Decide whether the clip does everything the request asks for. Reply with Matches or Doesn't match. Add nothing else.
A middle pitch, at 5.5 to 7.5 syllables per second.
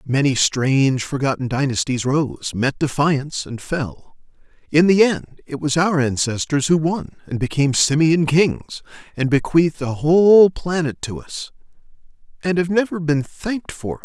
Doesn't match